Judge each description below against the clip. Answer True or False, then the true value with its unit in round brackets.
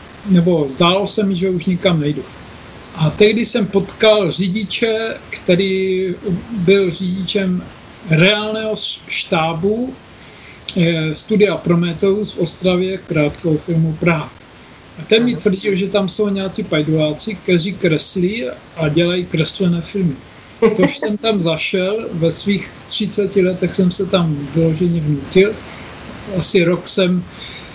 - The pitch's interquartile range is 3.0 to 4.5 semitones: True (3.3 semitones)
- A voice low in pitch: False (185 Hz)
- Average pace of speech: True (125 wpm)